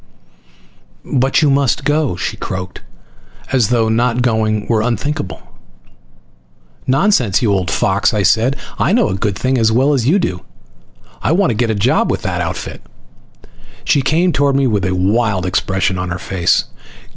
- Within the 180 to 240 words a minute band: No, average, 170 wpm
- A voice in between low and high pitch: No, low, 115 Hz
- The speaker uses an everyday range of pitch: No, wide, 5.8 semitones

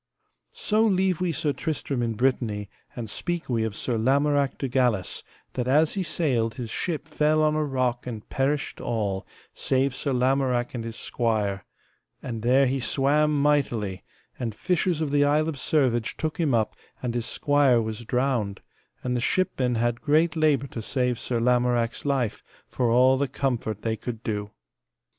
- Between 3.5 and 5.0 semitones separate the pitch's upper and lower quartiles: Yes, average, 4.0 semitones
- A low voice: Yes, low, 130 Hz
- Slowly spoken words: No, average, 175 wpm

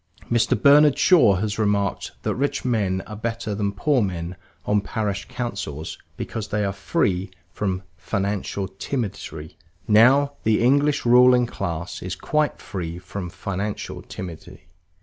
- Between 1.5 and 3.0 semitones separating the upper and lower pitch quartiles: No, average, 4.3 semitones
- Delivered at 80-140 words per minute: Yes, slow, 135 wpm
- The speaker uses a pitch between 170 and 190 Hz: No, low, 105 Hz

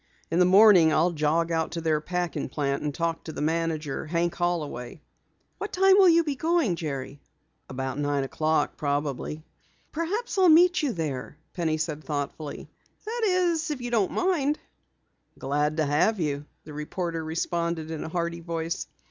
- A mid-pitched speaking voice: Yes, medium, 165 Hz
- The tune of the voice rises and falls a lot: Yes, wide, 6.6 semitones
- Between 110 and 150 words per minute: No, average, 165 wpm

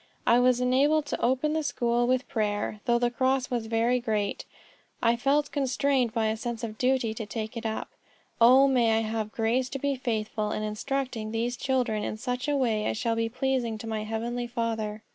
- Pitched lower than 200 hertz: No, high, 235 Hz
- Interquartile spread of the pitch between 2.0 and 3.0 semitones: Yes, average, 2.7 semitones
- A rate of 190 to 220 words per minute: Yes, average, 200 wpm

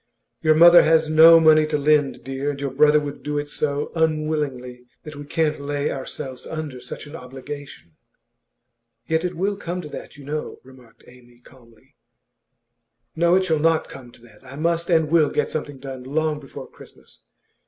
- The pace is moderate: Yes, average, 180 wpm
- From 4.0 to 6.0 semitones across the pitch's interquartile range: No, average, 2.9 semitones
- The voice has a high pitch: No, medium, 150 Hz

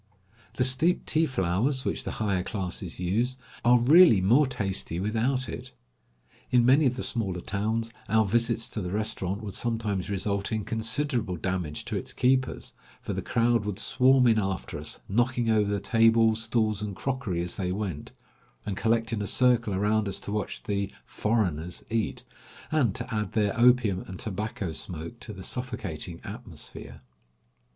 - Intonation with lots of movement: No, average, 3.7 semitones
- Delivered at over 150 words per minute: Yes, average, 165 wpm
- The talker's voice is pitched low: Yes, low, 110 Hz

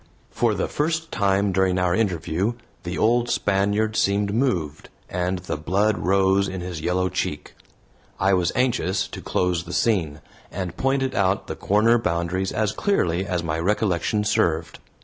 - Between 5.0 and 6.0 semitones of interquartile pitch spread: No, average, 3.3 semitones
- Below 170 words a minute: Yes, average, 155 wpm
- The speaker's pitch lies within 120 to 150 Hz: No, very low, 95 Hz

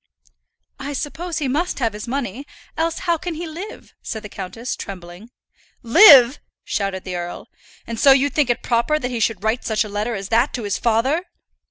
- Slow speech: No, average, 195 wpm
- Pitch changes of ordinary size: No, wide, 5.7 semitones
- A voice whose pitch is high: Yes, high, 240 Hz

